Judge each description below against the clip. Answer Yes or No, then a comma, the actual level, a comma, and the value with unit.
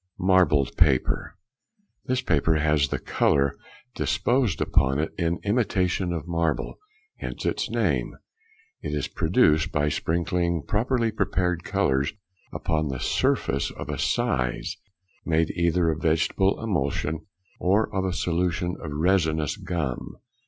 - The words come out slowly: Yes, slow, 130 wpm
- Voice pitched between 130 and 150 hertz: No, very low, 85 Hz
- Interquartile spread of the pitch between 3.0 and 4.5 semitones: Yes, average, 3.5 semitones